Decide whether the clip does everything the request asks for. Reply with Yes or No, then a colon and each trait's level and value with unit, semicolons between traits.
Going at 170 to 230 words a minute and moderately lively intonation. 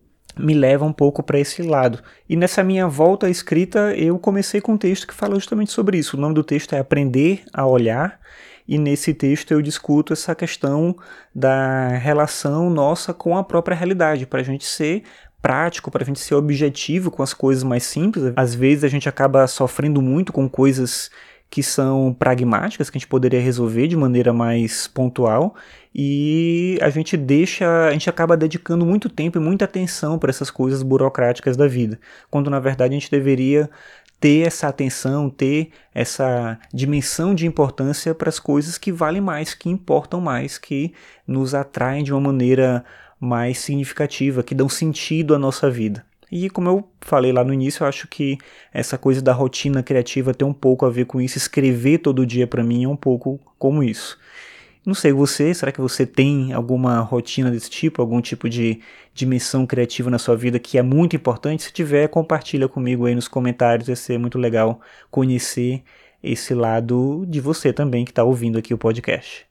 Yes: fast, 185 wpm; average, 3.8 semitones